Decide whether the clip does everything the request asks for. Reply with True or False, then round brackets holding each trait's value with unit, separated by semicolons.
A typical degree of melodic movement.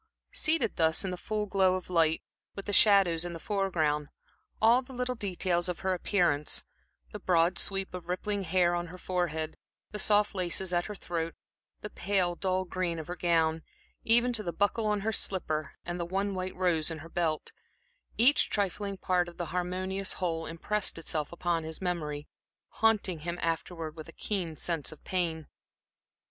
True (3.1 semitones)